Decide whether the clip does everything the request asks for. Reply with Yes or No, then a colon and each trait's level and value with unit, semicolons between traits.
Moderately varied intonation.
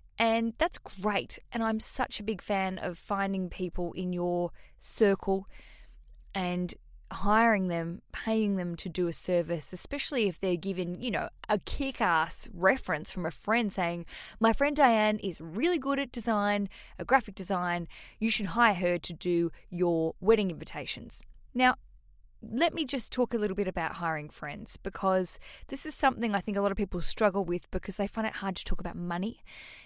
Yes: average, 4.1 semitones